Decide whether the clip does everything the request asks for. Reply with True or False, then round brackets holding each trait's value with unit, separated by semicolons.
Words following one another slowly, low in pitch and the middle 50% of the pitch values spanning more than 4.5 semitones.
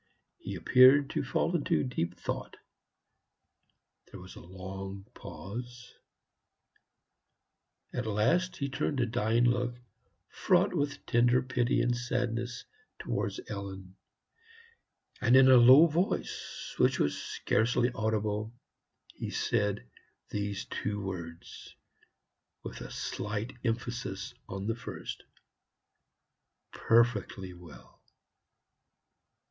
False (100 wpm; 115 Hz; 3.7 semitones)